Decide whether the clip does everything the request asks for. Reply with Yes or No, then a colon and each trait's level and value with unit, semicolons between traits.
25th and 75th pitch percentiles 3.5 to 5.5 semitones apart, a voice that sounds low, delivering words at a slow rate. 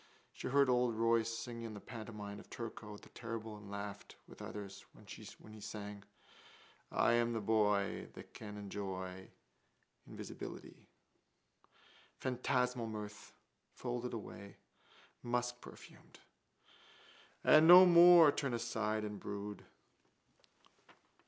No: average, 2.9 semitones; low, 110 Hz; slow, 110 wpm